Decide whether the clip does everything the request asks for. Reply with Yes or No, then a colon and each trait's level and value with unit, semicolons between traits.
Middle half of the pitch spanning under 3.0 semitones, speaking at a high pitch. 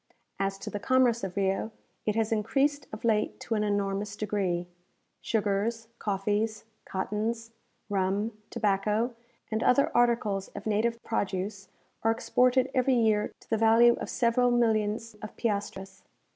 Yes: narrow, 2.5 semitones; high, 215 Hz